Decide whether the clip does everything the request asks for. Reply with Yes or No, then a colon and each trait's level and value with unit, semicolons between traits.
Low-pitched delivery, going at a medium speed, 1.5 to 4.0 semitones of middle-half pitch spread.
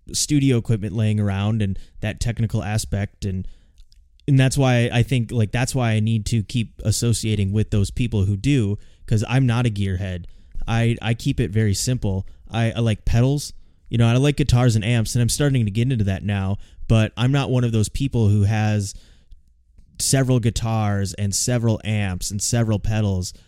Yes: low, 110 Hz; average, 190 wpm; average, 3.1 semitones